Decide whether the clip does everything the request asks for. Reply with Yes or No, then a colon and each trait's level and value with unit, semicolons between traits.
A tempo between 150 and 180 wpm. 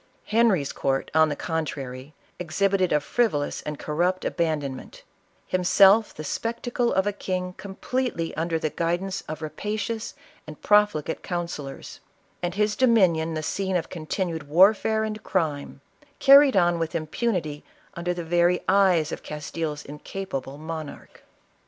No: average, 140 wpm